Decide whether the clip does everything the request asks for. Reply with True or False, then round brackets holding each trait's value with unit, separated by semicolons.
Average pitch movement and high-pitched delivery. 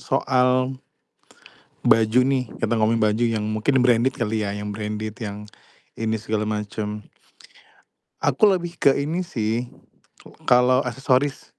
False (3.2 semitones; 115 Hz)